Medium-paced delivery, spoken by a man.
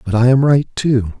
No: fast, 250 wpm; male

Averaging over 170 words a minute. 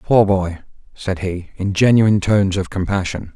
No: average, 160 wpm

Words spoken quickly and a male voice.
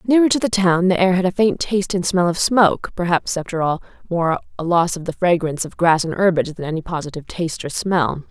No: fast, 240 wpm; female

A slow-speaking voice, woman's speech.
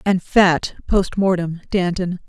Yes: slow, 105 wpm; female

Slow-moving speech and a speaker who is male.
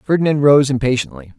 Yes: slow, 130 wpm; male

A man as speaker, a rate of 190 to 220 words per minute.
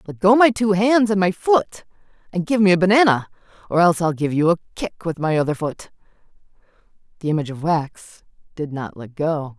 No: female; average, 200 wpm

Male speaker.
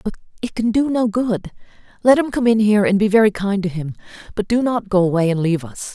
No: female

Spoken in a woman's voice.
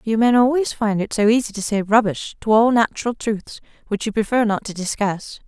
Yes: female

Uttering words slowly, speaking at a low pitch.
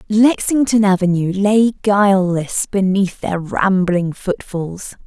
No: slow, 95 wpm; high, 195 Hz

